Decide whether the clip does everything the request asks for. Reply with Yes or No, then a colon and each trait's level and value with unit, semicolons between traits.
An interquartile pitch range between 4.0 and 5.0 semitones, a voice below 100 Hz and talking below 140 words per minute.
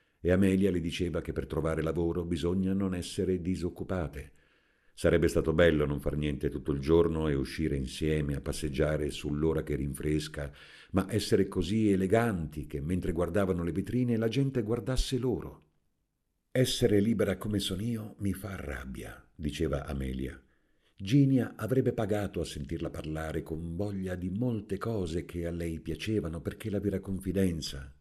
No: average, 4.6 semitones; very low, 85 Hz; average, 150 wpm